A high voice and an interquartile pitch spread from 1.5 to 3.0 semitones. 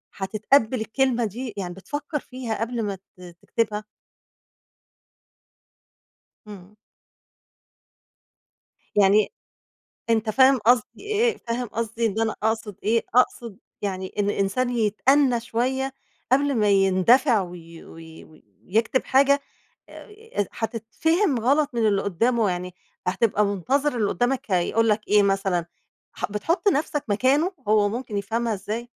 No: high, 225 Hz; average, 4.1 semitones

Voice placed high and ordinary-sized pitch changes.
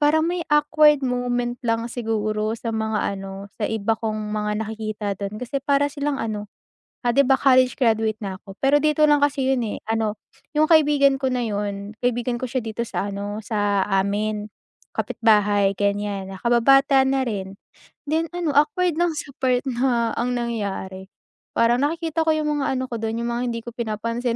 Yes: high, 235 Hz; average, 4.5 semitones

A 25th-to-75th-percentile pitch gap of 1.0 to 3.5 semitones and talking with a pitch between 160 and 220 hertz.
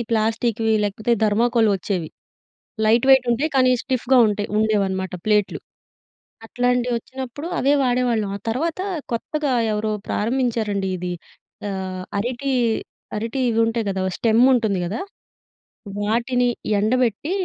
No: average, 3.1 semitones; high, 230 Hz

